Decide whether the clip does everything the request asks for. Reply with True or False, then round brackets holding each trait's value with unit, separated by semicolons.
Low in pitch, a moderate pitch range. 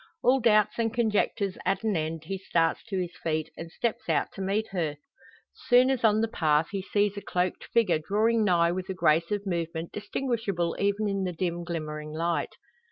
False (190 Hz; 4.1 semitones)